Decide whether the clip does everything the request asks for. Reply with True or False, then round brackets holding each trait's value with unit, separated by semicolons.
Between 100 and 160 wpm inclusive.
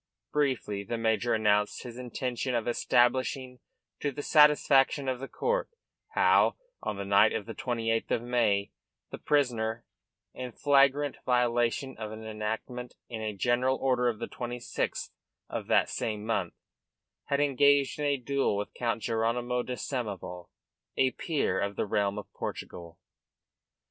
True (150 wpm)